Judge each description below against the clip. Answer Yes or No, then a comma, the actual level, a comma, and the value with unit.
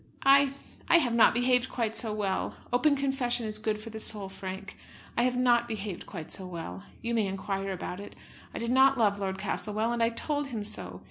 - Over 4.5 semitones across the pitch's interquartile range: No, average, 3.9 semitones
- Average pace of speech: No, fast, 210 wpm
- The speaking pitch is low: No, high, 220 Hz